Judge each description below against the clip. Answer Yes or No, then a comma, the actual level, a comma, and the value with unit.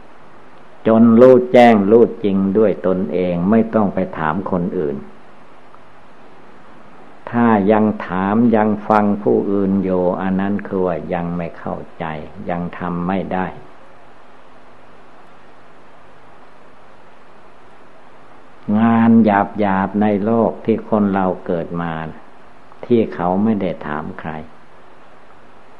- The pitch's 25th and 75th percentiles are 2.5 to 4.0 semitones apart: Yes, average, 3.4 semitones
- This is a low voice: Yes, very low, 95 Hz